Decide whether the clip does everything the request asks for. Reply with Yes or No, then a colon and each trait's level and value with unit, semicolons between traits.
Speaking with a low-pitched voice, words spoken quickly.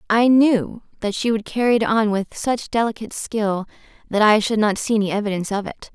No: high, 215 Hz; fast, 210 wpm